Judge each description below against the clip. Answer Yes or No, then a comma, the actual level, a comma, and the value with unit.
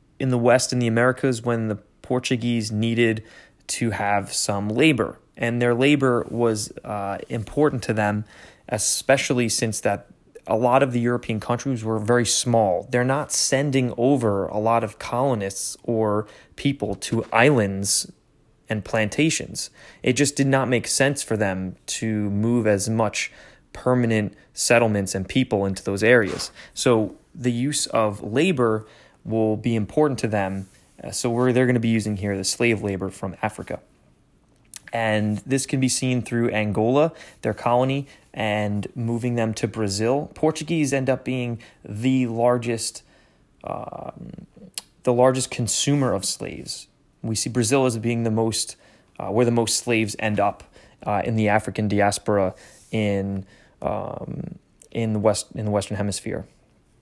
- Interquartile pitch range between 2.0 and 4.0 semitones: Yes, average, 3.2 semitones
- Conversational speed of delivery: Yes, average, 150 wpm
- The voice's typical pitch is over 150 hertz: No, low, 115 Hz